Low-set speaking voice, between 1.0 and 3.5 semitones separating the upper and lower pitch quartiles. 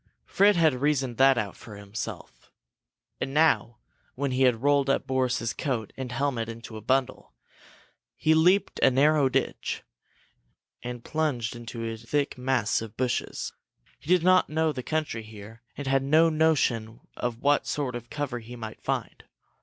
No: low, 130 Hz; average, 4.0 semitones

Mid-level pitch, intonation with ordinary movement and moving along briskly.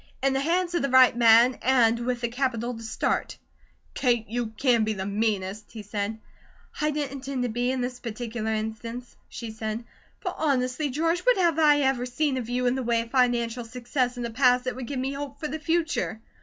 No: high, 245 Hz; average, 3.0 semitones; fast, 215 wpm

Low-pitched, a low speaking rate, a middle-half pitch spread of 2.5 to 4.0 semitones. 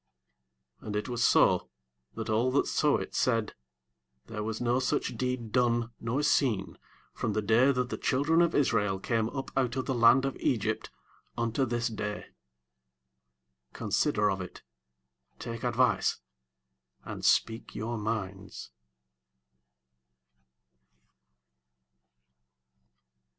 Yes: low, 115 Hz; slow, 120 wpm; average, 2.8 semitones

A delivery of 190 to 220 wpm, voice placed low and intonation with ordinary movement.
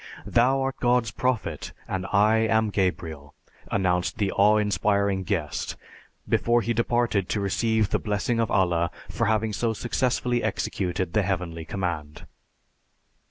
No: slow, 135 wpm; low, 105 Hz; average, 3.7 semitones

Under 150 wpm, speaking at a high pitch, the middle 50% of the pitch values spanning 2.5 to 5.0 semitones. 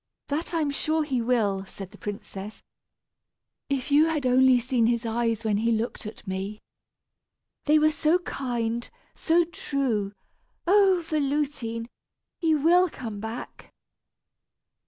No: slow, 135 wpm; very high, 255 Hz; wide, 5.4 semitones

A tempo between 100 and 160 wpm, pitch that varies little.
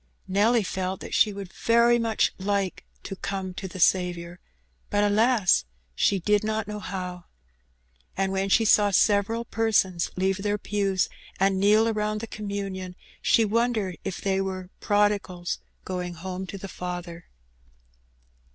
Yes: average, 145 wpm; narrow, 2.2 semitones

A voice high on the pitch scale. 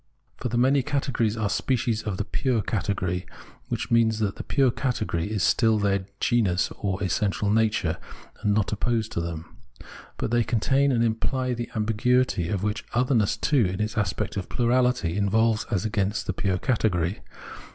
No: low, 110 Hz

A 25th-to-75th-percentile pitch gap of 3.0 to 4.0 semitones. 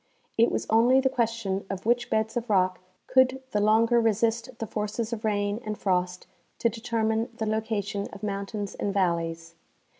No: narrow, 2.5 semitones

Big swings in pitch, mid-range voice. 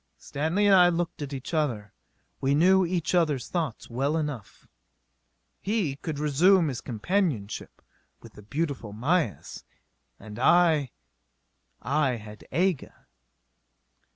Yes: wide, 5.7 semitones; medium, 150 Hz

